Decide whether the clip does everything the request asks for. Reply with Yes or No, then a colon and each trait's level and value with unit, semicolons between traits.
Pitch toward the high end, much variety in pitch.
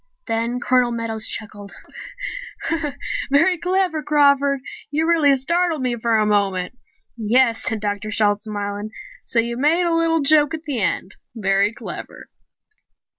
Yes: high, 240 Hz; wide, 6.0 semitones